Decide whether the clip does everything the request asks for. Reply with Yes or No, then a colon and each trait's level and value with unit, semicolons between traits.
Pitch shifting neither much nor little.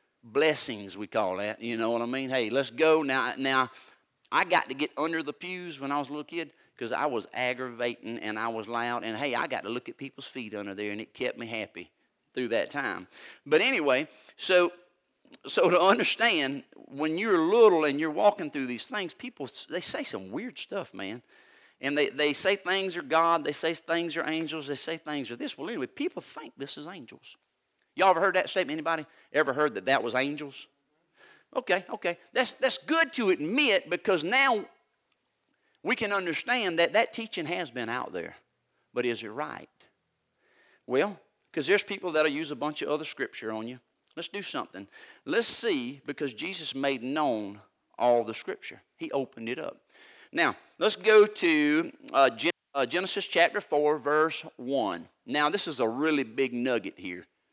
No: wide, 6.3 semitones